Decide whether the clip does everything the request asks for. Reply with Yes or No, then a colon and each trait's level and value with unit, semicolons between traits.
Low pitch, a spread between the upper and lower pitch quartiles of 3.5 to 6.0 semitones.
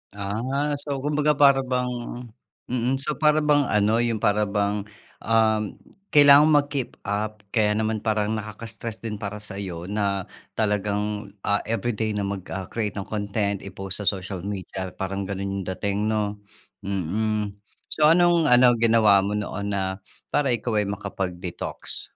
No: low, 105 Hz; average, 3.1 semitones